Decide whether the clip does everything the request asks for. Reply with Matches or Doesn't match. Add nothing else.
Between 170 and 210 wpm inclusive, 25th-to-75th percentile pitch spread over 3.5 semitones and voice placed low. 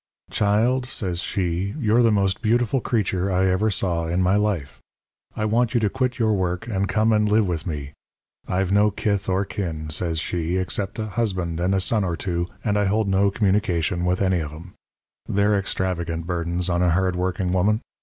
Doesn't match